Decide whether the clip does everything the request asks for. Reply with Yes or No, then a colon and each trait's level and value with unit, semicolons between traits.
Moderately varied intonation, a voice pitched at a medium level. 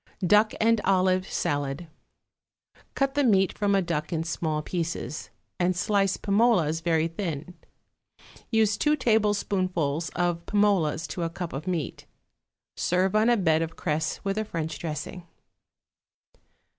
Yes: average, 4.1 semitones; medium, 180 Hz